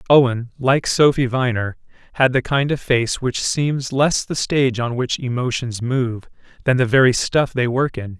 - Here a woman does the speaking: No, male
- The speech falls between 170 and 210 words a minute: Yes, average, 185 wpm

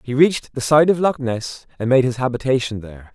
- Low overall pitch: Yes, low, 130 Hz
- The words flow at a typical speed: No, fast, 230 wpm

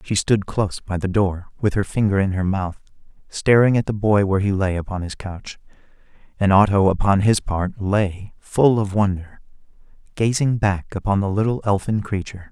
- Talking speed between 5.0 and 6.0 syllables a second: Yes, 5.1 syllables/s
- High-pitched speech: No, low, 100 Hz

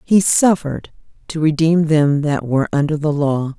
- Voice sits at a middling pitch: Yes, medium, 155 Hz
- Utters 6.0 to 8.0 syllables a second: No, 4.8 syllables/s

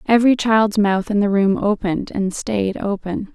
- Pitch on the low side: No, high, 205 Hz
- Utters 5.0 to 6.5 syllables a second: No, 4.7 syllables/s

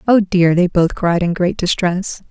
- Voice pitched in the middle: Yes, medium, 180 Hz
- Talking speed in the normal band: No, fast, 210 wpm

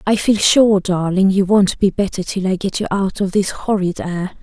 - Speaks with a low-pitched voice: No, high, 195 Hz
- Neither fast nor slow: No, fast, 230 wpm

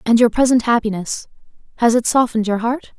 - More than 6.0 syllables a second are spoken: Yes, 6.2 syllables/s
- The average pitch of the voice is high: Yes, high, 230 Hz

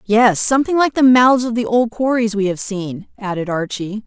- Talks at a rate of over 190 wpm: Yes, fast, 205 wpm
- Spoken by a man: No, female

